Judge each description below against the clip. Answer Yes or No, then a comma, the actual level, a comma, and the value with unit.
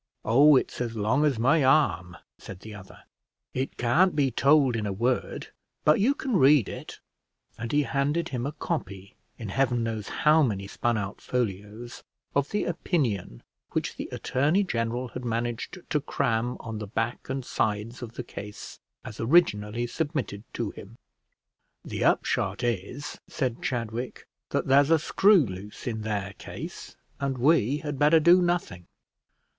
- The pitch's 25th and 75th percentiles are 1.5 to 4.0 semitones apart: No, average, 5.1 semitones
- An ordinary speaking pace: Yes, average, 160 wpm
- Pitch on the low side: Yes, low, 120 Hz